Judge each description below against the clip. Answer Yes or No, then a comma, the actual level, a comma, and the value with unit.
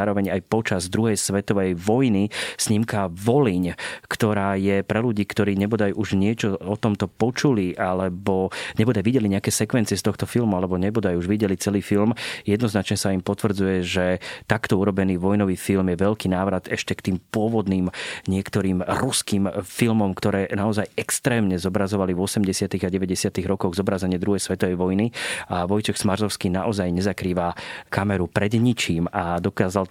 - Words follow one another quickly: No, average, 150 wpm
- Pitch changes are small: Yes, narrow, 2.2 semitones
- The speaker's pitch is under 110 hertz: Yes, low, 100 Hz